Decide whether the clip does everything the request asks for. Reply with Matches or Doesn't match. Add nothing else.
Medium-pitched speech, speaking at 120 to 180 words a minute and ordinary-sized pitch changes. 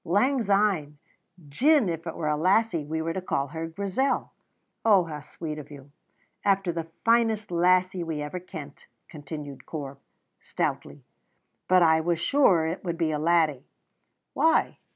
Matches